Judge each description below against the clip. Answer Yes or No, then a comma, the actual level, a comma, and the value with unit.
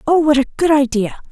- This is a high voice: Yes, very high, 285 Hz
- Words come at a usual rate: No, fast, 225 wpm